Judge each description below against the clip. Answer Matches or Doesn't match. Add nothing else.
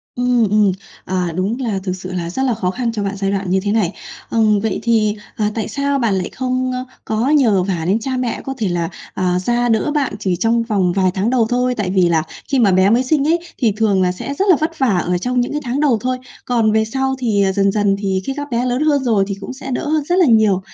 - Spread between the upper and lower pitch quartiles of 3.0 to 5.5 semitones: Matches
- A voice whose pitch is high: Matches